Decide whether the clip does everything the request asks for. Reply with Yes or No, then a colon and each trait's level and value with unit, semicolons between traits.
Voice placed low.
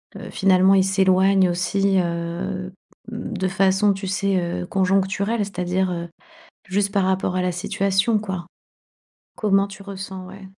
No: high, 190 Hz